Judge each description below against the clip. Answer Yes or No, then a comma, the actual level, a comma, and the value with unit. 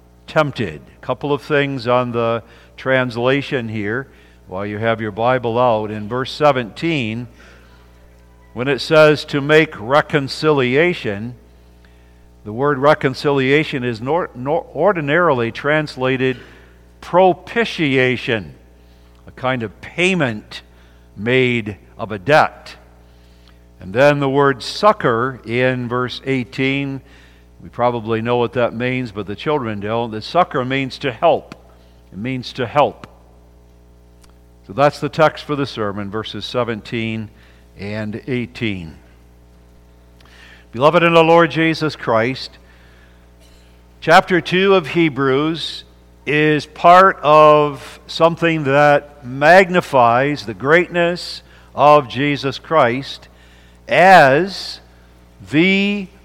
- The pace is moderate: No, slow, 110 wpm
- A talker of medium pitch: No, low, 120 Hz